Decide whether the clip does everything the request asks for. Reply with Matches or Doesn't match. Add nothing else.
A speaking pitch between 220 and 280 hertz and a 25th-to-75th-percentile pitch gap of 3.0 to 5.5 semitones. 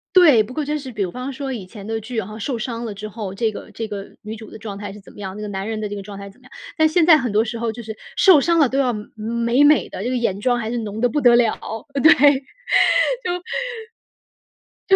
Matches